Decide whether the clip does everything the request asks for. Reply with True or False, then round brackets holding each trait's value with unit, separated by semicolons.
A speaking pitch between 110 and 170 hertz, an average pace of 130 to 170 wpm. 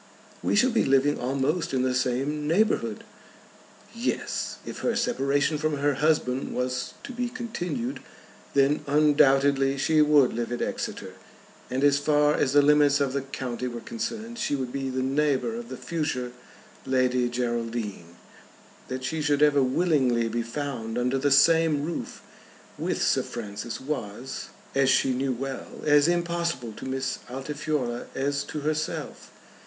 True (140 Hz; 150 wpm)